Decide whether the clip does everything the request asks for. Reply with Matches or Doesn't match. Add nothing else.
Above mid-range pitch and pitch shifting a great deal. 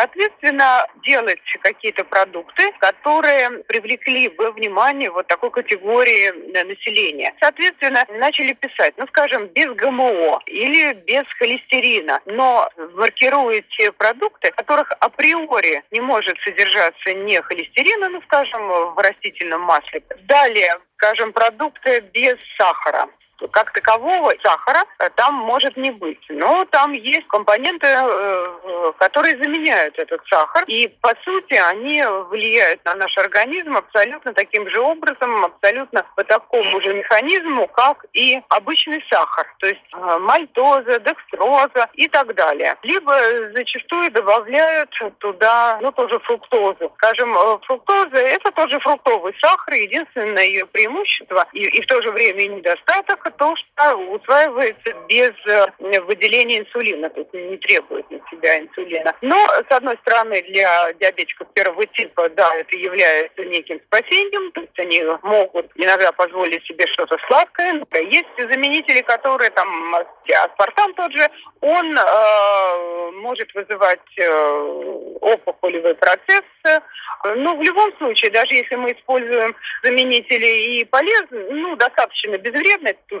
Matches